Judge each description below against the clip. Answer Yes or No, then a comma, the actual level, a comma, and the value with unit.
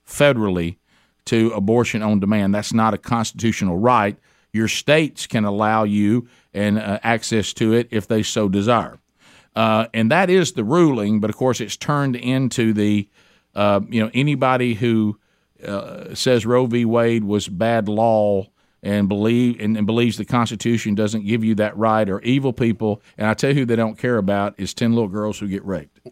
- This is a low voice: Yes, low, 110 Hz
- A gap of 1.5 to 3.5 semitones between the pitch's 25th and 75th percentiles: Yes, narrow, 2.5 semitones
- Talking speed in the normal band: Yes, average, 185 wpm